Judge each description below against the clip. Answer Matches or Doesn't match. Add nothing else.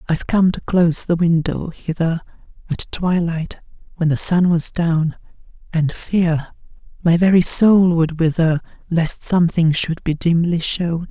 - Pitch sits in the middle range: Matches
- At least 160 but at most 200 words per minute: Doesn't match